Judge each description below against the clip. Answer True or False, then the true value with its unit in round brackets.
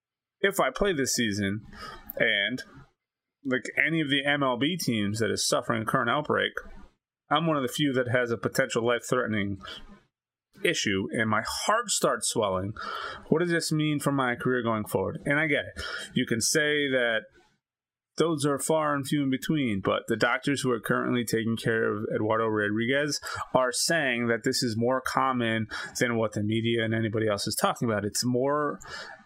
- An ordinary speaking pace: True (185 wpm)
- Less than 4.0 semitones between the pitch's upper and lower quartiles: False (4.3 semitones)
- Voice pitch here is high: False (125 Hz)